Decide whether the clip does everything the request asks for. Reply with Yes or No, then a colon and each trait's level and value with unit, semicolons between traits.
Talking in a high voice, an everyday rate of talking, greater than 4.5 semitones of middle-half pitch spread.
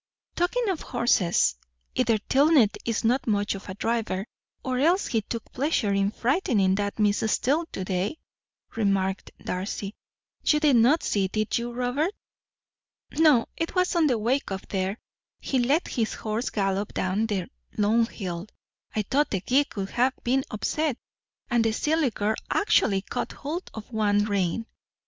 Yes: high, 225 Hz; average, 160 wpm; average, 5.2 semitones